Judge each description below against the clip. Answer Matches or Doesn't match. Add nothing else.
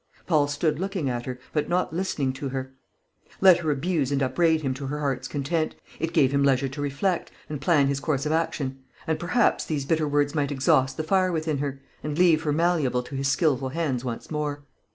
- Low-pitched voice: Doesn't match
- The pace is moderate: Doesn't match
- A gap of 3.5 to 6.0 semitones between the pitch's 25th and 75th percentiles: Doesn't match